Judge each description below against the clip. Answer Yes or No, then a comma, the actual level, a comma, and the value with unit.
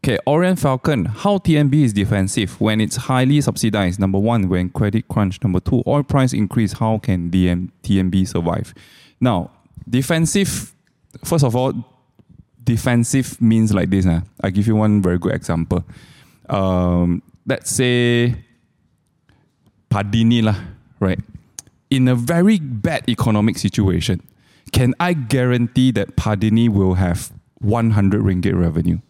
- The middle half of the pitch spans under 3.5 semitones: No, average, 4.9 semitones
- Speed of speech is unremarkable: No, slow, 130 wpm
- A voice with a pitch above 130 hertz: No, low, 110 Hz